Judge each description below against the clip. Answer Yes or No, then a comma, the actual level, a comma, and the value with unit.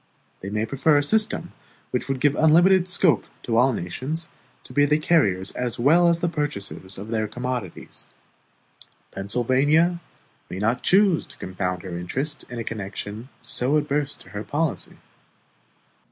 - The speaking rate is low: No, average, 155 wpm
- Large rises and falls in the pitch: Yes, wide, 6.7 semitones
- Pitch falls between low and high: No, low, 130 Hz